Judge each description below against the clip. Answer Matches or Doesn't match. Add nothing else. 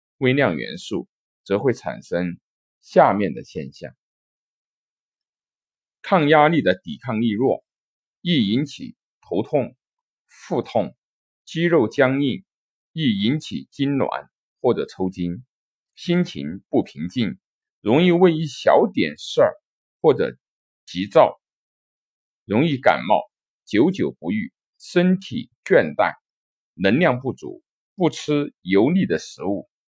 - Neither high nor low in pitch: Matches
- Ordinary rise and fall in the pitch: Doesn't match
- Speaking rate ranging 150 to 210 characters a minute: Matches